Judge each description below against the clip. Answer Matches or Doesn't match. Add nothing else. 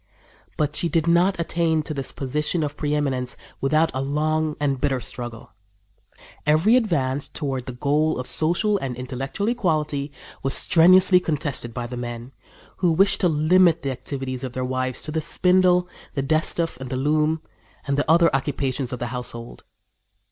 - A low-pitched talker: Doesn't match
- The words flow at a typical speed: Matches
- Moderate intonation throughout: Matches